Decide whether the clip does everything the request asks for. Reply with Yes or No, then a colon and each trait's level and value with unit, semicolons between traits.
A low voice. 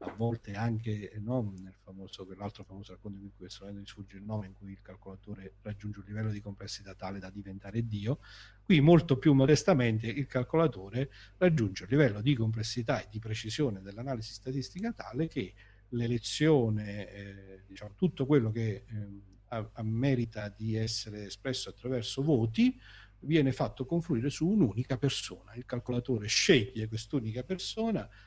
Yes: low, 110 Hz